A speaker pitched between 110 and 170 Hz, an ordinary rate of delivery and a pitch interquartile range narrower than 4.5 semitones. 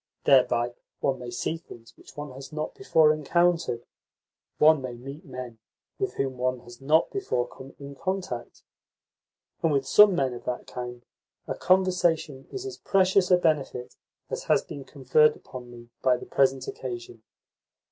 No: low, 135 Hz; average, 160 wpm; average, 4.8 semitones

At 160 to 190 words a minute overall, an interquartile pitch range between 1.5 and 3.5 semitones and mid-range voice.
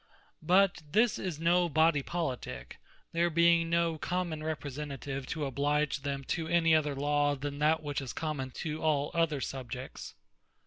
No: average, 150 wpm; average, 2.9 semitones; medium, 155 Hz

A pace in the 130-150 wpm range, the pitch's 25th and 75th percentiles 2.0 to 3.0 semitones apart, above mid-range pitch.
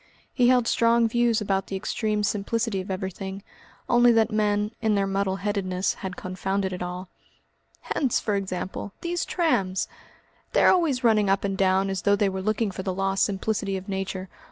No: average, 180 wpm; narrow, 2.4 semitones; high, 200 Hz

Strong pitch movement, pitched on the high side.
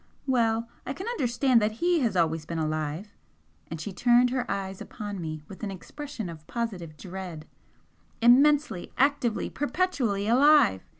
Yes: wide, 6.9 semitones; high, 220 Hz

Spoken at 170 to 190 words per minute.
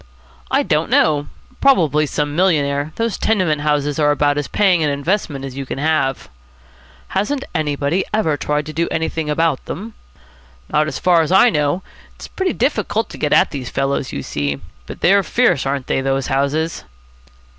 Yes: average, 175 wpm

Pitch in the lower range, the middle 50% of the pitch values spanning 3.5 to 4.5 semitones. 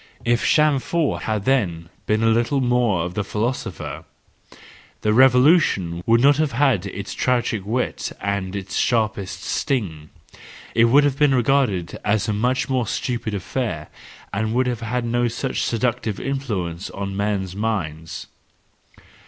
Yes: low, 115 Hz; average, 4.2 semitones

